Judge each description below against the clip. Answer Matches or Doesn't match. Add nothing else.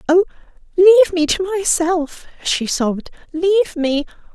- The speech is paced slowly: Matches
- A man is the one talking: Doesn't match